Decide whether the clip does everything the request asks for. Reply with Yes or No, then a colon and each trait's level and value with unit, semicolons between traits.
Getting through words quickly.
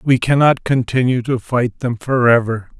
No: average, 150 wpm